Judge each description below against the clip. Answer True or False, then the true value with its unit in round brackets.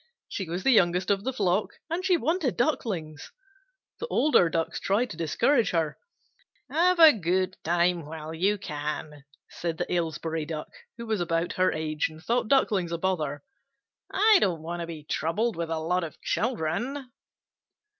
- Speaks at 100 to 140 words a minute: False (165 wpm)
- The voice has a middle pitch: True (175 Hz)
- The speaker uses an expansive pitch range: True (6.4 semitones)